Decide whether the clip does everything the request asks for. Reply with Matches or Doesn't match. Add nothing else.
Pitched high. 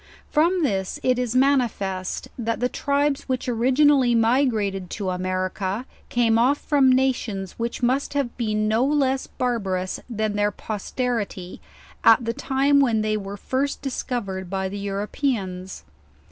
Matches